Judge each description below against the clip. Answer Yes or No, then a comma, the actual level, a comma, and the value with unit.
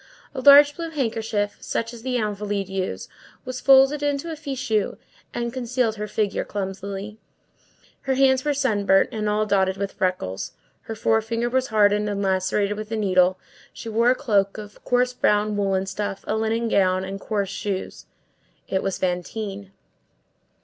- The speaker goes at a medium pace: Yes, average, 160 wpm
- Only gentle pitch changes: No, average, 3.9 semitones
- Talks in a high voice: Yes, high, 215 Hz